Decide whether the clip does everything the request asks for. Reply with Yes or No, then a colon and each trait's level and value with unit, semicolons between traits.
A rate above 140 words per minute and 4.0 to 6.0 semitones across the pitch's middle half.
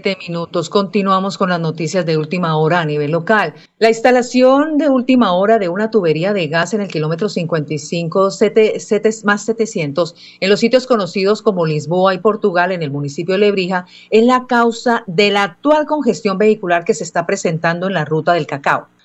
Yes: average, 185 wpm; average, 4.4 semitones